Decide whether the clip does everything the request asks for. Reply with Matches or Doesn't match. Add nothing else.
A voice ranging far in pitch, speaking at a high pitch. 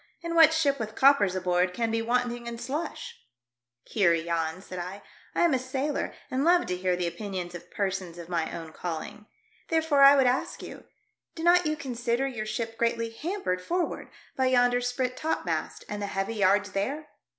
Matches